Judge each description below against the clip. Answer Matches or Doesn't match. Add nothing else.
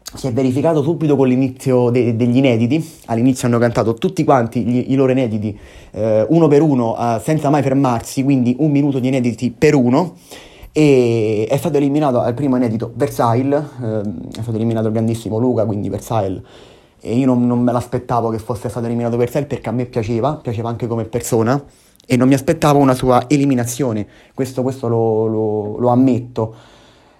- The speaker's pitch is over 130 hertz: Doesn't match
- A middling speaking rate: Doesn't match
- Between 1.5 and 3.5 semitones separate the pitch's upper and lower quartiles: Matches